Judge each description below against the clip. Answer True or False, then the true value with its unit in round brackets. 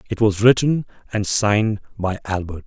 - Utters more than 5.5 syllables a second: False (4.9 syllables/s)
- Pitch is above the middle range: False (105 Hz)